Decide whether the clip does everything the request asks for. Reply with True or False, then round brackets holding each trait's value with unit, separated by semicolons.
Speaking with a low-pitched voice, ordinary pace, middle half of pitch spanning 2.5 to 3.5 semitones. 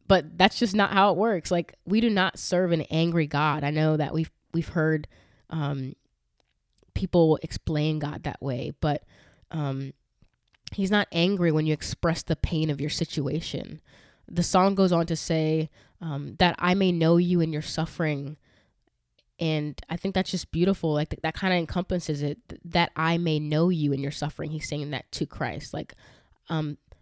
False (160 Hz; 180 wpm; 2.8 semitones)